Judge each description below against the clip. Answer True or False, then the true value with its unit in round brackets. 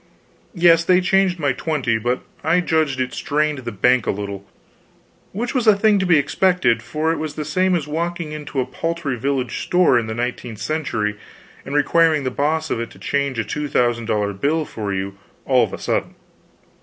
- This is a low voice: False (145 Hz)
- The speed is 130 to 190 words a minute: False (200 wpm)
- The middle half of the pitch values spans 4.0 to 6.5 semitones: True (5.6 semitones)